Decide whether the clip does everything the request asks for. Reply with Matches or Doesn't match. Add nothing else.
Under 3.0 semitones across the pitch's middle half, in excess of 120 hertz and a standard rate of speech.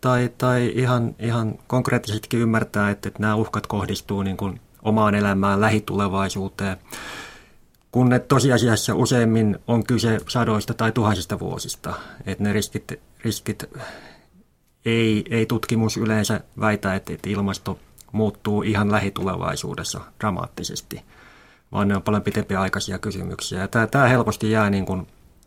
Doesn't match